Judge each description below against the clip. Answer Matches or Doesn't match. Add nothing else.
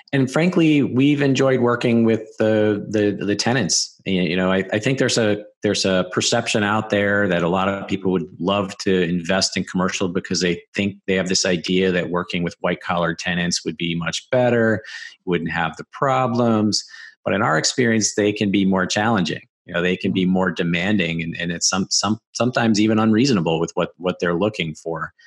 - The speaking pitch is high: Doesn't match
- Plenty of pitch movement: Doesn't match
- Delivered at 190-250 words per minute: Matches